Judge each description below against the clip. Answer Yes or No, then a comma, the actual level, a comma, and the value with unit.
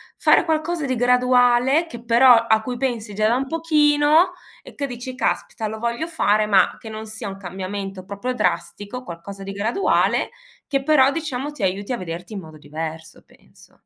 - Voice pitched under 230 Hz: No, high, 235 Hz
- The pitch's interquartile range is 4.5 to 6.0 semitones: Yes, average, 5.1 semitones